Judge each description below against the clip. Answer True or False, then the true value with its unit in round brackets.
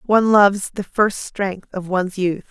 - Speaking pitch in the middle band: False (195 Hz)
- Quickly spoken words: False (190 wpm)